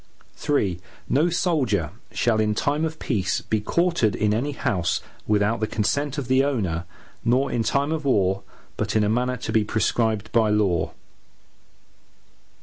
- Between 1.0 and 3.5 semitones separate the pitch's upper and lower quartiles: No, average, 5.2 semitones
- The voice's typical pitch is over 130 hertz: No, low, 115 Hz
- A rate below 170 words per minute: Yes, average, 155 wpm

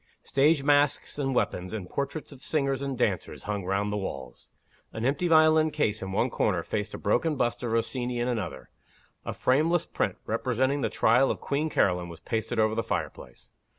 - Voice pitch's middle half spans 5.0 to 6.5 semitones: Yes, average, 5.3 semitones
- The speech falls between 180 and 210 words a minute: Yes, average, 185 wpm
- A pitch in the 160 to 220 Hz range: No, low, 125 Hz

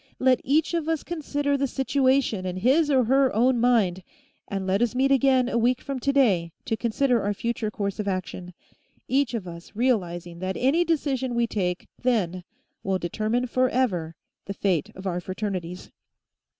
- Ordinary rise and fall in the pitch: No, wide, 6.0 semitones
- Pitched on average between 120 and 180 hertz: No, high, 235 Hz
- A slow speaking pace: No, average, 170 wpm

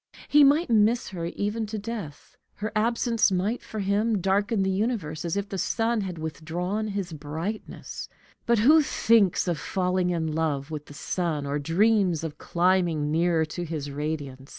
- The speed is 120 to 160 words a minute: No, average, 170 wpm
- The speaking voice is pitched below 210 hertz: Yes, medium, 185 Hz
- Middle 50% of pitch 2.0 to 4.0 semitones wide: No, average, 5.2 semitones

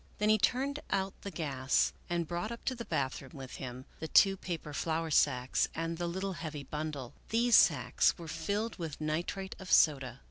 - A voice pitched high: No, medium, 165 Hz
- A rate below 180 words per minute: No, average, 185 wpm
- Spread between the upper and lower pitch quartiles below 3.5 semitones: No, average, 5.1 semitones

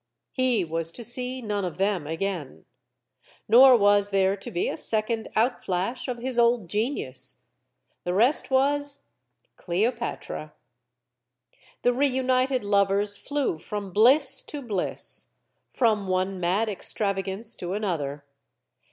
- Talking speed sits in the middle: No, slow, 120 wpm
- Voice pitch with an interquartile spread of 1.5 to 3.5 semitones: No, average, 4.7 semitones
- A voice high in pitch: Yes, high, 210 Hz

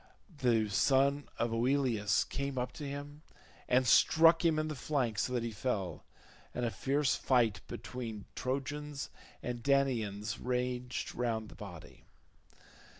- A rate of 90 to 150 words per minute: Yes, average, 140 wpm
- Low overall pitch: Yes, low, 125 Hz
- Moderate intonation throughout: Yes, average, 3.4 semitones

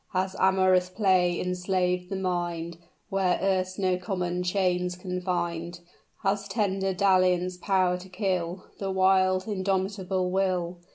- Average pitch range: No, narrow, 1.1 semitones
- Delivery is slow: Yes, slow, 120 wpm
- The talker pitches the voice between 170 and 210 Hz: Yes, medium, 185 Hz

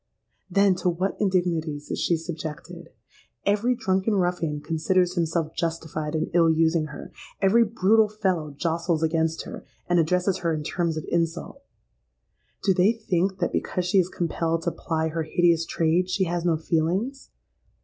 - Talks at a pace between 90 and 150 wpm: No, average, 160 wpm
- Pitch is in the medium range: Yes, medium, 170 Hz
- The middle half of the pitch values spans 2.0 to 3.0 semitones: Yes, narrow, 2.5 semitones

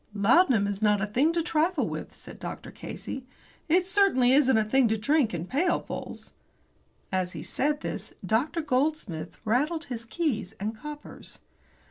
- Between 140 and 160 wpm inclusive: Yes, average, 155 wpm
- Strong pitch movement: Yes, wide, 6.5 semitones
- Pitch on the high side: Yes, very high, 260 Hz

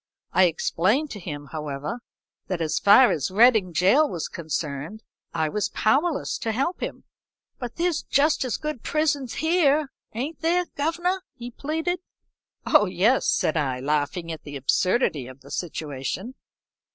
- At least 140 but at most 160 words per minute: Yes, average, 150 wpm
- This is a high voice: Yes, high, 215 Hz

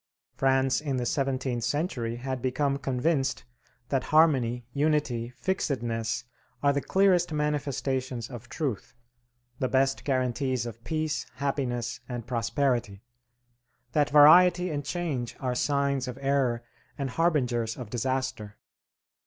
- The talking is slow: Yes, slow, 120 wpm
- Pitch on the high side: No, low, 135 Hz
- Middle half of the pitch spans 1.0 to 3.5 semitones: Yes, average, 3.1 semitones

